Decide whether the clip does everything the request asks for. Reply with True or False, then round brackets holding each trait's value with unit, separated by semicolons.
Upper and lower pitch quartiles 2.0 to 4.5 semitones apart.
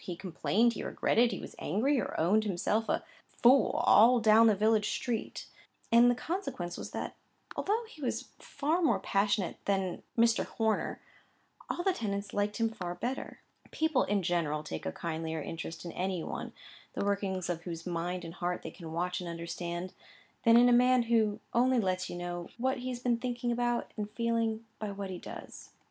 False (5.1 semitones)